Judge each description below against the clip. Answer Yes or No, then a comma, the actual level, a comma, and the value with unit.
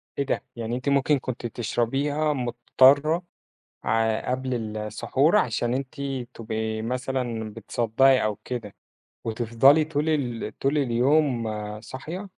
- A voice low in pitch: Yes, low, 125 Hz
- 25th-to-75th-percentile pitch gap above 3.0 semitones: Yes, average, 3.6 semitones